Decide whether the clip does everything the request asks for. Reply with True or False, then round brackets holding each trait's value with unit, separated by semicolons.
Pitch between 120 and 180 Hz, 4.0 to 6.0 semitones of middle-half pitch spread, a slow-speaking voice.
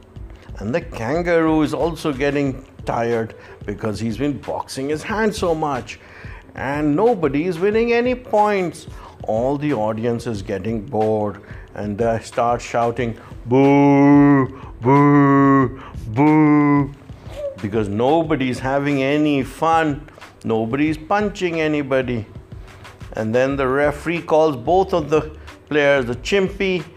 True (135 Hz; 5.4 semitones; 120 wpm)